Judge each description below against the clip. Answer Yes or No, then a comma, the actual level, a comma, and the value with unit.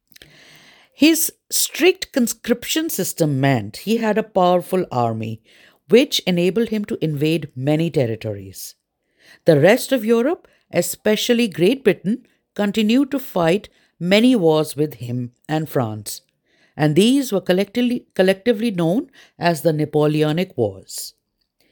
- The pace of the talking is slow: Yes, slow, 115 wpm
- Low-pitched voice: No, medium, 185 Hz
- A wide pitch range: Yes, wide, 7.6 semitones